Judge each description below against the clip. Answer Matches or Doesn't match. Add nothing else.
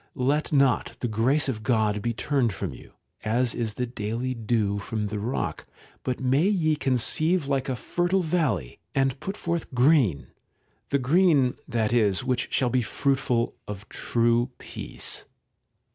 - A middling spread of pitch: Matches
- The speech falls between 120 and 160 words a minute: Matches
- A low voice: Matches